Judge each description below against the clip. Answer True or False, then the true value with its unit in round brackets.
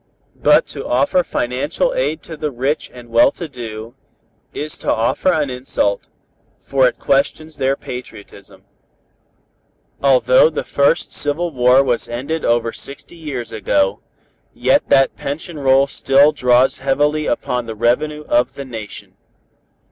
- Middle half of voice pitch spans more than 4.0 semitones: False (3.7 semitones)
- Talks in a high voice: False (135 Hz)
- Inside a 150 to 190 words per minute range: False (140 wpm)